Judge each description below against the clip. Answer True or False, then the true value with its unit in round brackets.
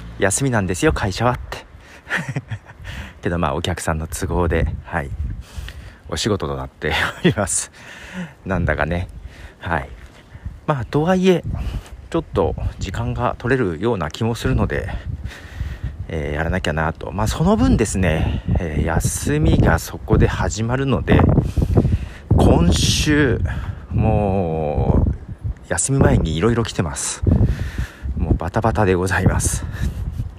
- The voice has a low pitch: True (95 Hz)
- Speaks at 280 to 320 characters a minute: False (225 characters per minute)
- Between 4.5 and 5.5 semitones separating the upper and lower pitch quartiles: True (5.1 semitones)